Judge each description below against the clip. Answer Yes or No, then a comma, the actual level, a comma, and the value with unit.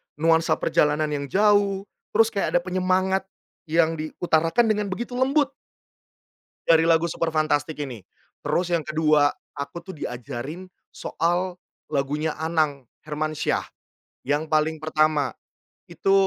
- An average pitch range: Yes, average, 3.5 semitones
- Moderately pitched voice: Yes, medium, 160 Hz